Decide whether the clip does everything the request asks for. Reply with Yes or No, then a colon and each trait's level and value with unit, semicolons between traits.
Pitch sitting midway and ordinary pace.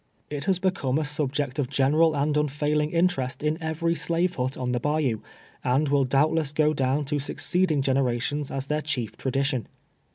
Yes: medium, 145 Hz; average, 175 wpm